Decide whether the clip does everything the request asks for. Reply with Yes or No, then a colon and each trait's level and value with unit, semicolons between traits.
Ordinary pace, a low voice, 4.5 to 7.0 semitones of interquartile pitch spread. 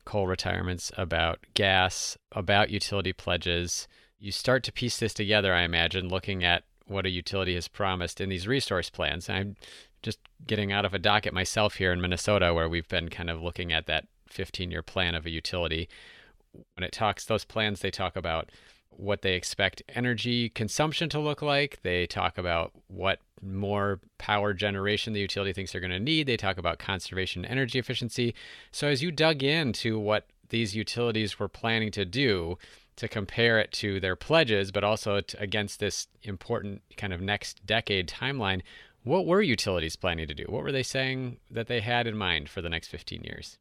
No: average, 190 wpm; low, 100 Hz; average, 3.8 semitones